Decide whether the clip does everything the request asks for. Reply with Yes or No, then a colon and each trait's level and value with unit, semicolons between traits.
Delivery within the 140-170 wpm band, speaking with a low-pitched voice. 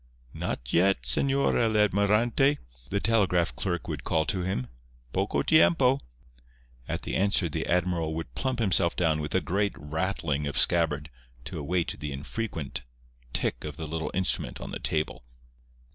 Yes: average, 150 wpm; very low, 85 Hz